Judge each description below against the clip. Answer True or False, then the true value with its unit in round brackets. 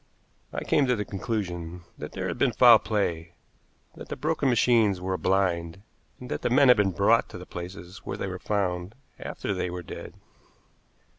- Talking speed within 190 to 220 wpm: True (195 wpm)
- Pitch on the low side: True (95 Hz)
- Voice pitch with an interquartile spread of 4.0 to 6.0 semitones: True (4.4 semitones)